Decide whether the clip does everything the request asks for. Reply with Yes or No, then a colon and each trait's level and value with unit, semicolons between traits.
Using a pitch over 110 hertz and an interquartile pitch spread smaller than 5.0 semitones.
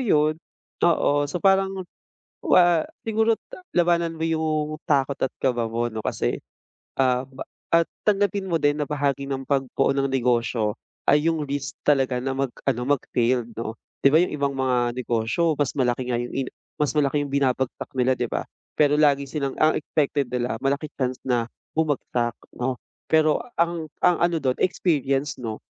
Yes: medium, 140 Hz; average, 3.7 semitones